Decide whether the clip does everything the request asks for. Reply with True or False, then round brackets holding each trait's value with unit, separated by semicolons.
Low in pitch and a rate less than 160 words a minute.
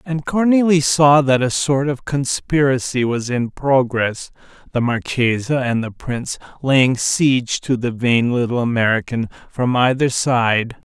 True (130 Hz; 140 wpm)